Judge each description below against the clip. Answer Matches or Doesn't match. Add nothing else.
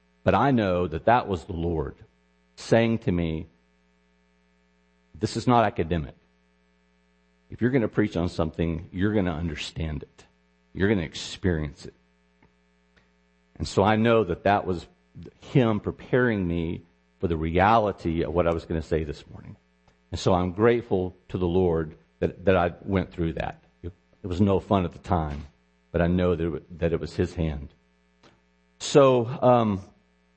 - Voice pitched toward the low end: Matches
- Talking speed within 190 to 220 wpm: Doesn't match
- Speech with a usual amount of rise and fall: Doesn't match